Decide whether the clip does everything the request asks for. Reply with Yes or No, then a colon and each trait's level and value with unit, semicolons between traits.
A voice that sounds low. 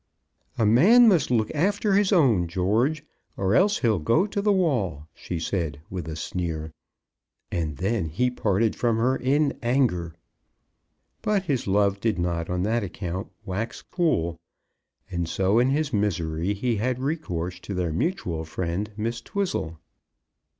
Yes: low, 105 Hz